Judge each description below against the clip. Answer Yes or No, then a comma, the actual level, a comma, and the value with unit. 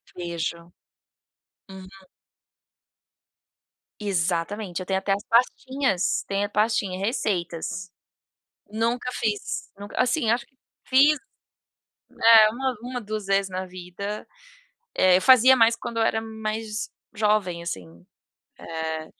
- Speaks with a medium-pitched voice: No, high, 205 Hz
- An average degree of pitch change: Yes, average, 3.9 semitones